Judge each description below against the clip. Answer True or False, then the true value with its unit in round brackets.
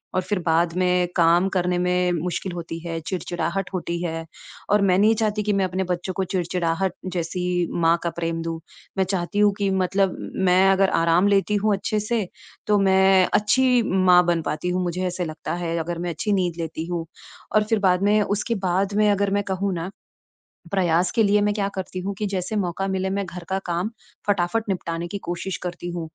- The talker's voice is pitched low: False (185 Hz)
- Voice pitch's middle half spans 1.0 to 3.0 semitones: True (2.4 semitones)